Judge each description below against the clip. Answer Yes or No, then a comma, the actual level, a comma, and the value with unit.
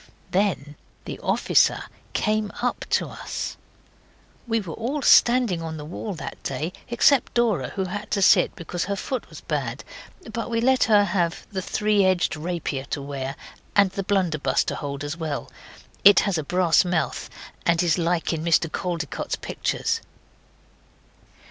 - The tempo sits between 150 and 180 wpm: Yes, average, 160 wpm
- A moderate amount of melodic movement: Yes, average, 4.5 semitones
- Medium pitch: Yes, medium, 180 Hz